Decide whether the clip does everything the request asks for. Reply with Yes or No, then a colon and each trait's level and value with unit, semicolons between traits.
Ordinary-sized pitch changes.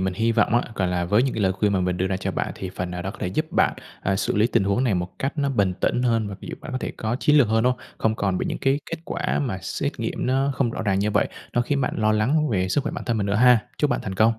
Yes: average, 4.8 semitones